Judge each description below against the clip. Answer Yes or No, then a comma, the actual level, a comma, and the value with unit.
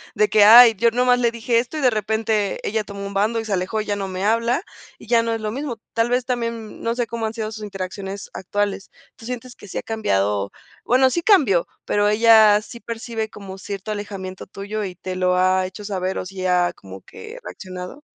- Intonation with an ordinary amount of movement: Yes, average, 3.2 semitones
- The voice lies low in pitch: No, high, 215 Hz